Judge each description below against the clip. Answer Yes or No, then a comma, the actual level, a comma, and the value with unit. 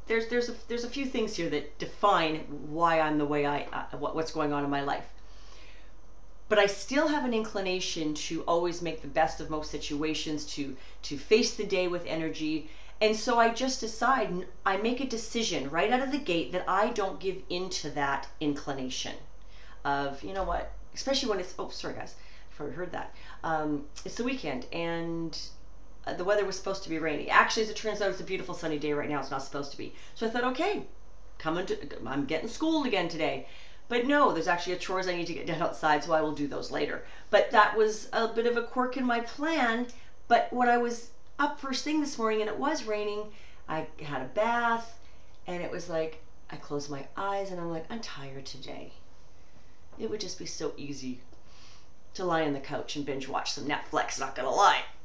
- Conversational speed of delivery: No, fast, 215 wpm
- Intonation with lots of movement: Yes, wide, 7.0 semitones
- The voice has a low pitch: No, medium, 180 Hz